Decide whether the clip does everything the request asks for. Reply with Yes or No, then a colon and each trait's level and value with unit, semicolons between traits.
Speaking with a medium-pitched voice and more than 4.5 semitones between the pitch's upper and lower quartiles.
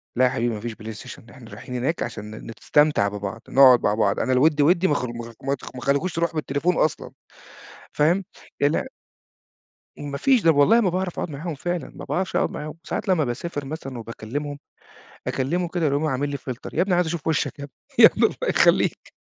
Yes: medium, 145 Hz; average, 4.9 semitones